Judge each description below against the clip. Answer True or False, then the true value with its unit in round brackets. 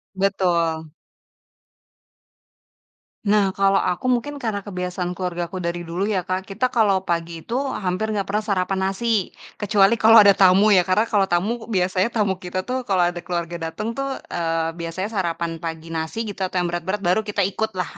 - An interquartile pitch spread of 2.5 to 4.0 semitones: True (2.8 semitones)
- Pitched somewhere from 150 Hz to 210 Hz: True (185 Hz)